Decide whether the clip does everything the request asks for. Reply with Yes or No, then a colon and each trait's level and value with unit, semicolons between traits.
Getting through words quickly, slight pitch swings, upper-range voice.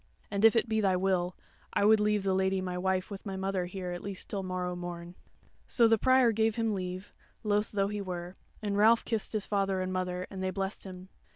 Yes: fast, 225 wpm; narrow, 2.2 semitones; high, 195 Hz